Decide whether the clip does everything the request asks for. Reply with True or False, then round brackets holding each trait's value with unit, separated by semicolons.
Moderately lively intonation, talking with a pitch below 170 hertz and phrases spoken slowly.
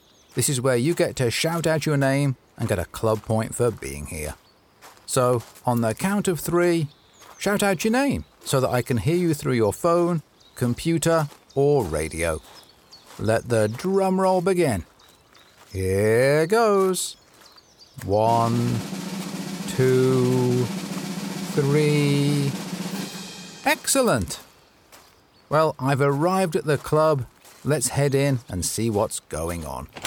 False (7.9 semitones; 140 Hz; 130 wpm)